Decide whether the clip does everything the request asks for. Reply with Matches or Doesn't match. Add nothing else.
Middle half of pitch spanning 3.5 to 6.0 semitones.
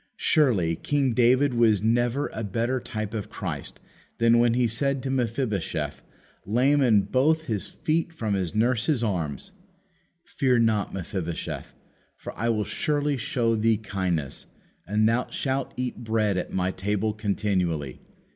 Matches